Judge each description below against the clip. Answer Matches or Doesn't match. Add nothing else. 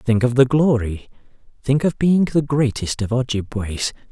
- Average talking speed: Matches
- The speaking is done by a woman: Doesn't match